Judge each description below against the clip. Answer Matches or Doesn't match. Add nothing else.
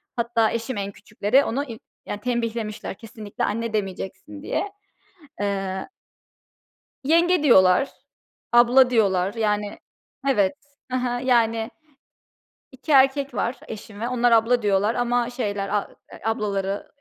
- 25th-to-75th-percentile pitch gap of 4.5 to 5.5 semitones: Doesn't match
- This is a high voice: Matches